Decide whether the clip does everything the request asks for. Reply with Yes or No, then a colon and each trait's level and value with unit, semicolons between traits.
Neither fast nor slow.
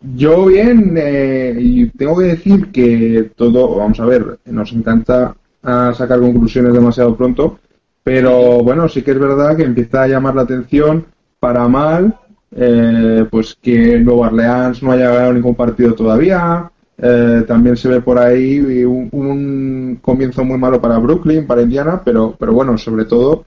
Yes: average, 160 wpm